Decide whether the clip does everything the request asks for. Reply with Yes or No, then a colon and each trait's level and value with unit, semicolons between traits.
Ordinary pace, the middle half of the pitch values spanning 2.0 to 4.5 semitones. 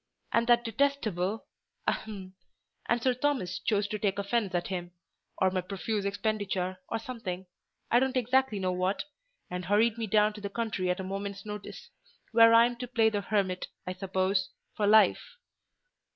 Yes: average, 150 wpm; average, 3.7 semitones